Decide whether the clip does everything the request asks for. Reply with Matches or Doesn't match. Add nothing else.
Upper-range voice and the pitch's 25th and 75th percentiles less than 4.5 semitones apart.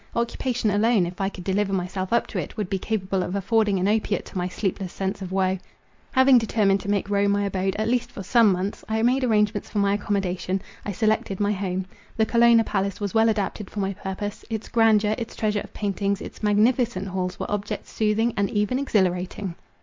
Matches